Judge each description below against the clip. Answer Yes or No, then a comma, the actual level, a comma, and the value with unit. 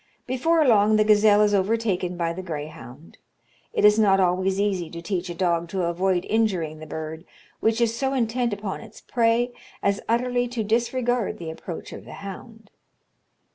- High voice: Yes, high, 205 Hz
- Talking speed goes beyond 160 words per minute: Yes, average, 175 wpm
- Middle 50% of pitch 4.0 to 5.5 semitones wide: Yes, average, 4.5 semitones